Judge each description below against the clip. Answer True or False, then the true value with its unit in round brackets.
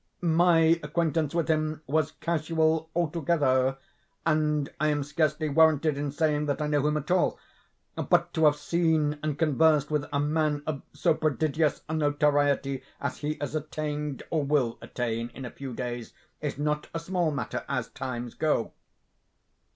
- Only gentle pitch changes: True (1.9 semitones)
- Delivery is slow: False (160 wpm)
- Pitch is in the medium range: True (150 Hz)